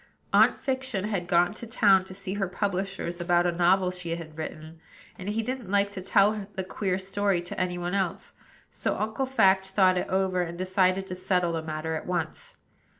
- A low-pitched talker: No, medium, 185 Hz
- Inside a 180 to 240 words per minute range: Yes, average, 200 wpm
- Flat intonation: Yes, narrow, 2.2 semitones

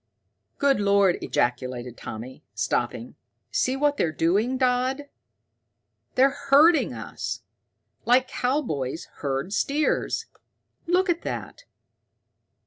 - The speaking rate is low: Yes, slow, 95 wpm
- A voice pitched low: No, very high, 250 Hz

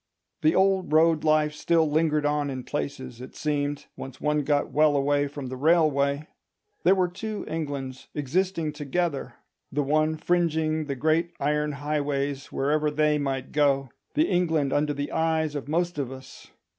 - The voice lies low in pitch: No, medium, 150 Hz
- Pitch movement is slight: Yes, narrow, 2.1 semitones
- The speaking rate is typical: Yes, average, 155 wpm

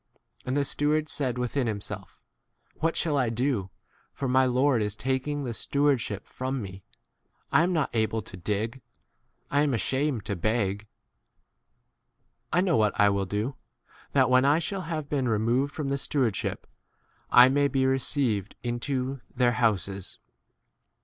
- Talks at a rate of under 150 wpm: No, average, 155 wpm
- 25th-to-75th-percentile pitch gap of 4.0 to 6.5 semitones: Yes, average, 4.4 semitones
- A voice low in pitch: Yes, low, 130 Hz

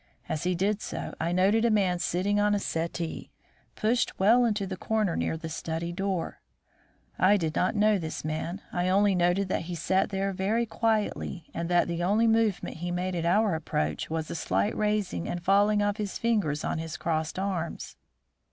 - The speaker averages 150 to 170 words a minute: No, average, 190 wpm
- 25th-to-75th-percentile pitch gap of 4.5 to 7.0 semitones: No, average, 3.6 semitones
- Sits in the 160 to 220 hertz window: Yes, medium, 185 Hz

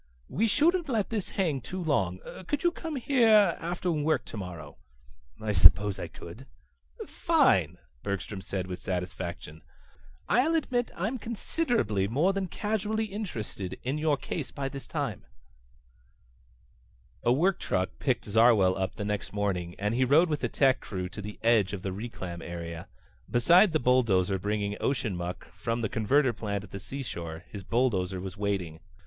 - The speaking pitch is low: Yes, low, 115 Hz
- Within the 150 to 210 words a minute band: Yes, average, 160 wpm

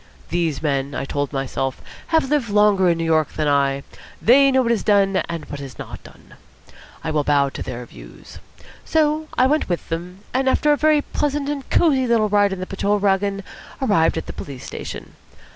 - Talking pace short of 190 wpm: No, average, 200 wpm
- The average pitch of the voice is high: Yes, high, 195 Hz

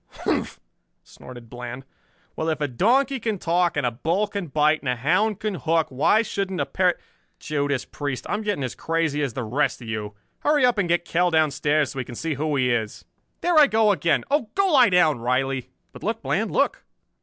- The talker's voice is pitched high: No, medium, 155 Hz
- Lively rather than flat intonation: Yes, wide, 7.3 semitones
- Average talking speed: No, fast, 210 wpm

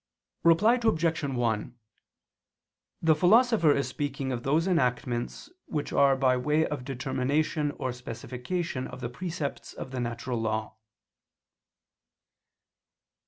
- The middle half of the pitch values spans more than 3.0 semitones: Yes, average, 4.4 semitones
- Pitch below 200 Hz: Yes, medium, 140 Hz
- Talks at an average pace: No, slow, 115 wpm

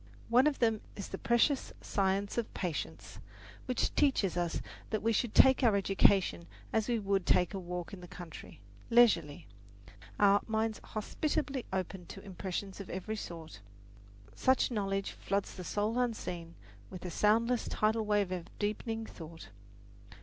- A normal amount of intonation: Yes, average, 3.9 semitones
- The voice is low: No, high, 200 Hz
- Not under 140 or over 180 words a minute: Yes, average, 150 wpm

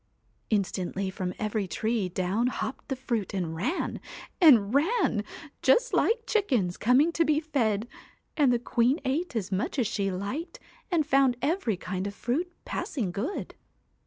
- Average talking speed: Yes, average, 155 wpm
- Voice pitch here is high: Yes, high, 240 Hz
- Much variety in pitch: Yes, wide, 7.2 semitones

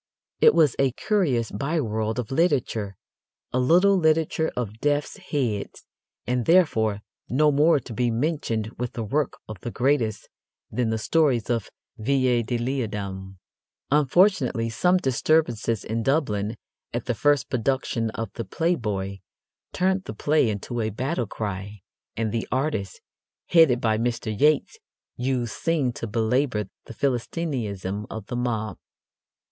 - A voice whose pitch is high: No, low, 120 Hz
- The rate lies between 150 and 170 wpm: No, average, 140 wpm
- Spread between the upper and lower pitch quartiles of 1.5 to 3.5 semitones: No, average, 4.9 semitones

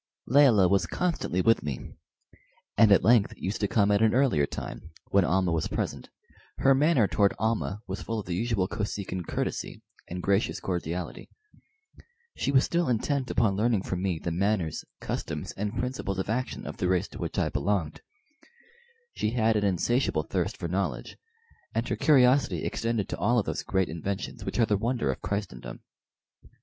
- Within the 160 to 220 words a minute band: Yes, average, 175 wpm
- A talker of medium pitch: No, low, 105 Hz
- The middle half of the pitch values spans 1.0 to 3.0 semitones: No, average, 4.2 semitones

